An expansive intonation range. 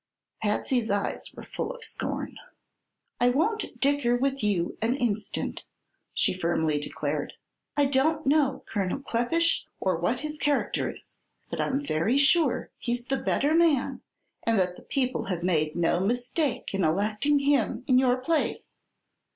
Yes: wide, 6.1 semitones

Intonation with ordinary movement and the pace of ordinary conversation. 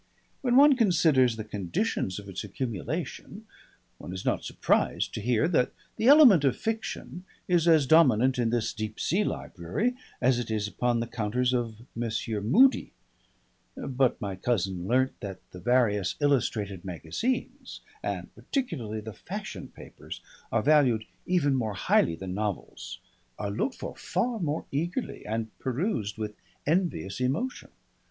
No: wide, 7.1 semitones; average, 145 wpm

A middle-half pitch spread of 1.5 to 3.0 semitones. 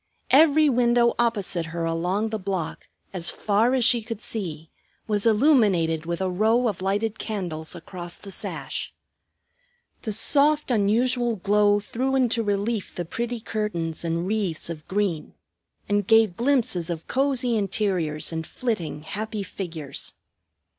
No: average, 5.2 semitones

